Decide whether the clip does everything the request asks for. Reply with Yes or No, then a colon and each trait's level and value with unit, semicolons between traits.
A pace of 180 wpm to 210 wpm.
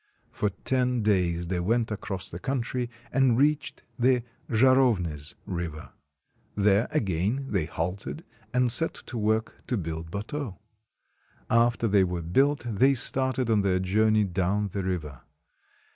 No: slow, 135 wpm